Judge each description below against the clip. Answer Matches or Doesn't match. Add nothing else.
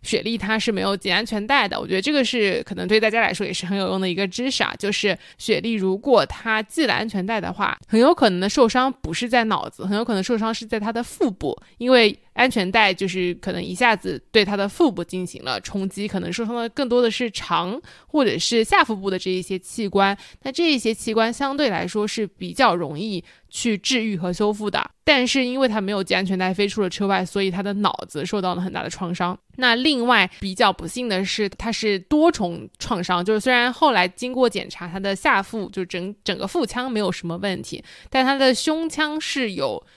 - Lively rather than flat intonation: Doesn't match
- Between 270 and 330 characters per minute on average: Matches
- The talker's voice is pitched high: Matches